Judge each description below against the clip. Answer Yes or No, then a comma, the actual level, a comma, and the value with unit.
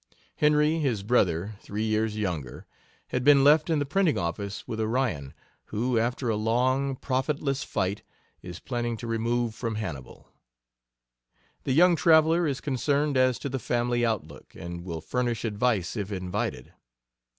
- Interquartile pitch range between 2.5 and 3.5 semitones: No, average, 4.7 semitones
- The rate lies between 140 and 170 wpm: Yes, average, 150 wpm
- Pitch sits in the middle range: No, low, 120 Hz